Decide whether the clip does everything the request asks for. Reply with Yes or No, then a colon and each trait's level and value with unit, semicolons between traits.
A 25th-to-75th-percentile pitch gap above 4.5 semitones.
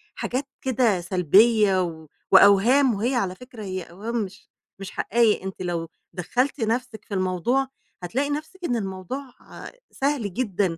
Yes: average, 5.3 semitones